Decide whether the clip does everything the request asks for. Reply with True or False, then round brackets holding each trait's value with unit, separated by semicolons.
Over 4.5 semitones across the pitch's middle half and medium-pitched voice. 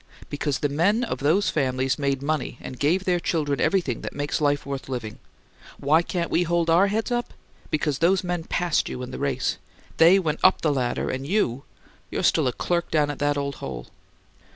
False (4.0 semitones; 150 Hz)